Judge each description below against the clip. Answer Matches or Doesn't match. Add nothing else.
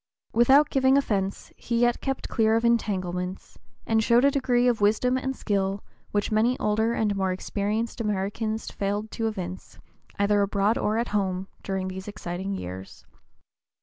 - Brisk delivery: Doesn't match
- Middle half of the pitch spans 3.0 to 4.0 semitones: Matches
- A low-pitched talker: Doesn't match